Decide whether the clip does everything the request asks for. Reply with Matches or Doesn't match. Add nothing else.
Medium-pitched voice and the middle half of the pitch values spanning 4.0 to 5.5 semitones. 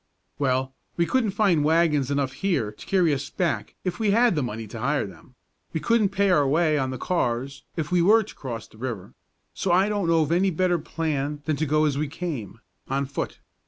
Matches